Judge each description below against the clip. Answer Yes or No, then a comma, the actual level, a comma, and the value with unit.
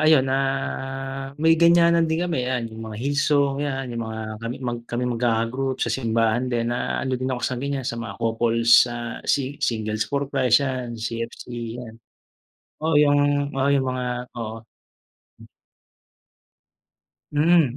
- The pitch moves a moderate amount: Yes, average, 3.4 semitones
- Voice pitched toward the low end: Yes, low, 130 Hz